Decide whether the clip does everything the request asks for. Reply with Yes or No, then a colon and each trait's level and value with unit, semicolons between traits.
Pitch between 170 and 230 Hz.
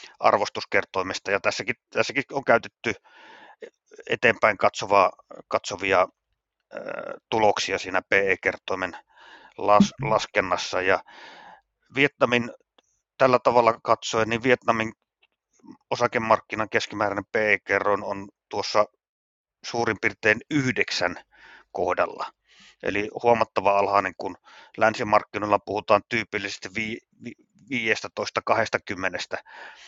No: low, 110 Hz